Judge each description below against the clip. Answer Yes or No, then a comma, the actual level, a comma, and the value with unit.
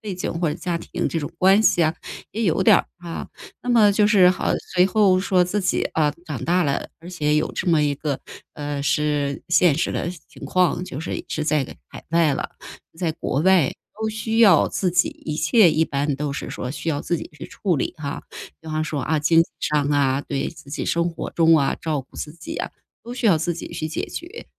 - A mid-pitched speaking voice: Yes, medium, 165 Hz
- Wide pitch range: No, average, 3.6 semitones